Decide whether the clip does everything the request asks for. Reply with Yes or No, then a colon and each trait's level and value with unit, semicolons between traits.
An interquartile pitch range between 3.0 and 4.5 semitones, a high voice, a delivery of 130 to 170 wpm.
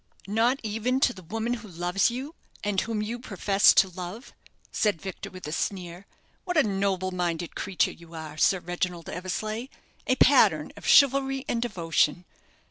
No: average, 4.9 semitones; high, 195 Hz; average, 165 wpm